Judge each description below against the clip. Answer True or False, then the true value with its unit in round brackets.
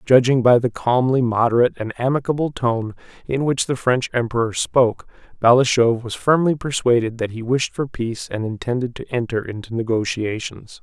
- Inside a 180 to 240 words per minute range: False (160 wpm)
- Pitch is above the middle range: False (120 Hz)